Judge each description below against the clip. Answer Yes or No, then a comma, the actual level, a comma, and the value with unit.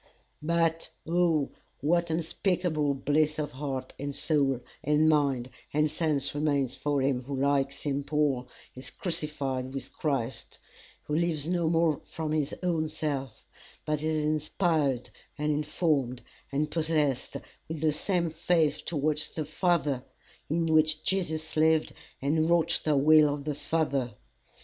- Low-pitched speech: No, medium, 150 Hz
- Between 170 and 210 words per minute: No, average, 140 wpm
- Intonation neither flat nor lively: No, narrow, 2.3 semitones